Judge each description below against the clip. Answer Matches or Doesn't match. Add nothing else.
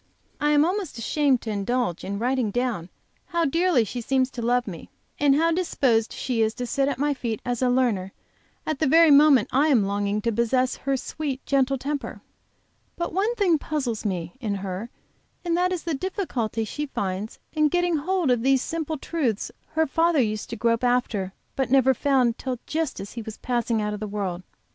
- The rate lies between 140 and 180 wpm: Doesn't match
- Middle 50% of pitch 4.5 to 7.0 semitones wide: Matches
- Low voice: Doesn't match